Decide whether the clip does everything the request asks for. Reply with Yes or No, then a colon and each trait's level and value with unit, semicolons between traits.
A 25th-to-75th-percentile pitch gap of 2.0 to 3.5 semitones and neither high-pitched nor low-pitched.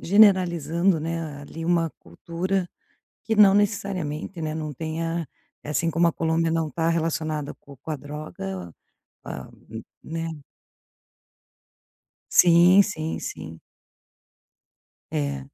Yes: narrow, 2.4 semitones; medium, 165 Hz